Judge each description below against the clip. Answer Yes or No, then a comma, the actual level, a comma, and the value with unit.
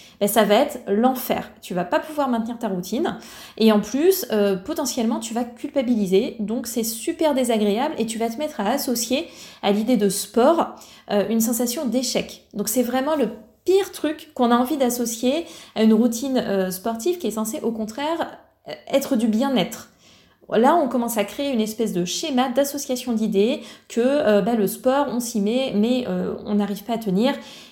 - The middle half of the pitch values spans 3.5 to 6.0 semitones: Yes, average, 3.9 semitones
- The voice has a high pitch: Yes, high, 235 Hz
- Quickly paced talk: No, average, 195 wpm